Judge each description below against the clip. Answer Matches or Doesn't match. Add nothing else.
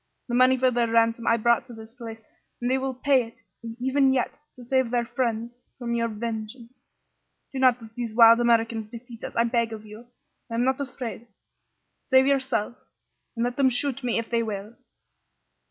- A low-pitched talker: Doesn't match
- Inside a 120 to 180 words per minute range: Doesn't match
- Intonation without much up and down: Matches